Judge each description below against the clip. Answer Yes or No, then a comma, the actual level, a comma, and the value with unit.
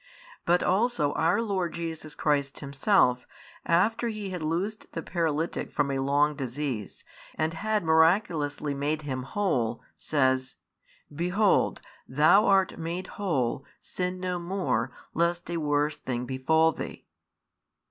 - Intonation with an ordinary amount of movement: Yes, average, 4.4 semitones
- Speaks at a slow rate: Yes, slow, 125 wpm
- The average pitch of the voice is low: No, medium, 160 Hz